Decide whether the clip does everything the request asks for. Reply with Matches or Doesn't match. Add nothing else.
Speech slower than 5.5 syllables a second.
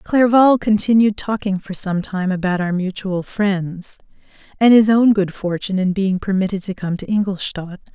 Matches